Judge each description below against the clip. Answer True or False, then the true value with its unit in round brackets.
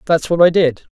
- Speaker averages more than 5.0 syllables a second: True (5.6 syllables/s)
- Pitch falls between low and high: True (165 Hz)